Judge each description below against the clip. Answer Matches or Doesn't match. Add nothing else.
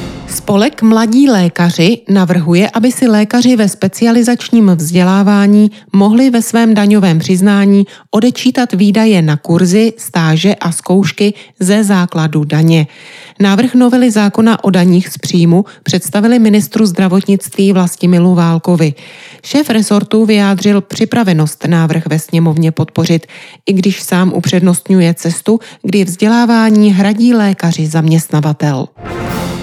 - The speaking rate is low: Matches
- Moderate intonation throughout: Matches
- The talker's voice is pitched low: Doesn't match